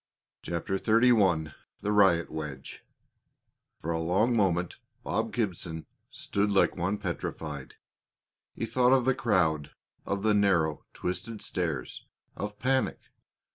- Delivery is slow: Yes, slow, 120 wpm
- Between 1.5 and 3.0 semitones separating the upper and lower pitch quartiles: No, average, 4.8 semitones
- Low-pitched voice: Yes, very low, 95 Hz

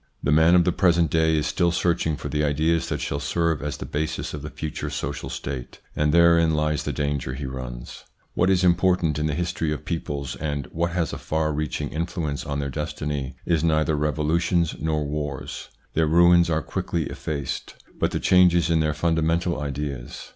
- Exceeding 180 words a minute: Yes, average, 190 wpm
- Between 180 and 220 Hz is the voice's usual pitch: No, very low, 75 Hz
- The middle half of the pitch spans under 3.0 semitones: Yes, narrow, 2.5 semitones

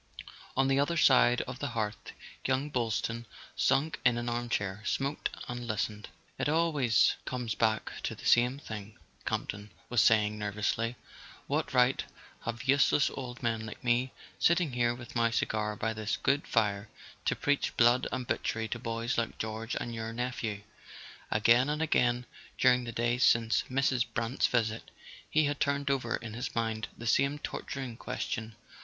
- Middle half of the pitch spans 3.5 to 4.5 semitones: No, average, 2.8 semitones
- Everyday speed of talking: Yes, average, 165 wpm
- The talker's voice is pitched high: No, low, 120 Hz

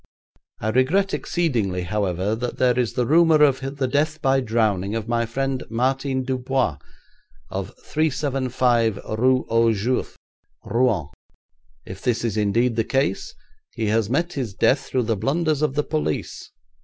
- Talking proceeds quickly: No, average, 150 wpm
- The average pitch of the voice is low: Yes, low, 125 Hz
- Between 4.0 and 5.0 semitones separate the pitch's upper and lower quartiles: No, average, 3.5 semitones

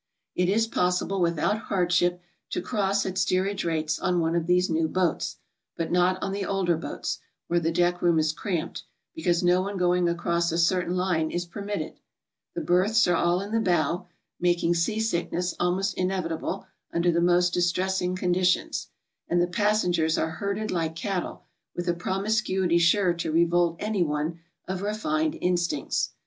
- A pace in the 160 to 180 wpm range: Yes, average, 170 wpm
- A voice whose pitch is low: No, medium, 180 Hz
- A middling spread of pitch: No, narrow, 1.9 semitones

